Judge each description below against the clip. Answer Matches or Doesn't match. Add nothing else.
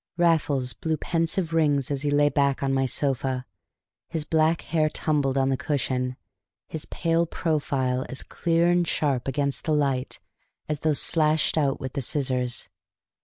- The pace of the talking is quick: Doesn't match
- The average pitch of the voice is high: Doesn't match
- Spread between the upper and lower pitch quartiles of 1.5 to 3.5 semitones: Matches